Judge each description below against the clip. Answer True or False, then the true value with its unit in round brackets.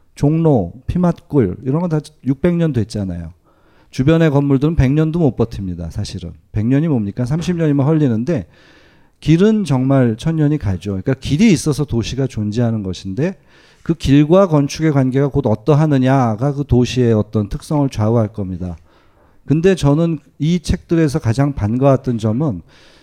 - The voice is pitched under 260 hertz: True (135 Hz)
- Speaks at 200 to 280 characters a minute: False (310 characters per minute)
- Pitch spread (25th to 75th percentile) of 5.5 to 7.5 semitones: True (5.9 semitones)